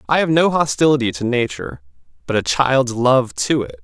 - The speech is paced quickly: No, average, 190 wpm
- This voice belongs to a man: Yes, male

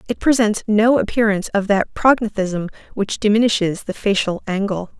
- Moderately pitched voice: No, high, 210 Hz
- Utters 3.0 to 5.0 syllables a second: No, 5.2 syllables/s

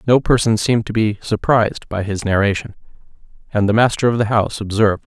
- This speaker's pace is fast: No, average, 185 wpm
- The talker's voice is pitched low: Yes, low, 110 Hz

